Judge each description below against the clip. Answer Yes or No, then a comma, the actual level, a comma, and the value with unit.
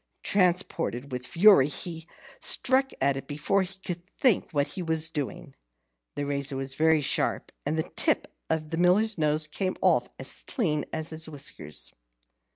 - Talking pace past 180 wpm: No, average, 160 wpm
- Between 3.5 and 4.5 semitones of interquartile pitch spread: Yes, average, 4.0 semitones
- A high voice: No, medium, 160 Hz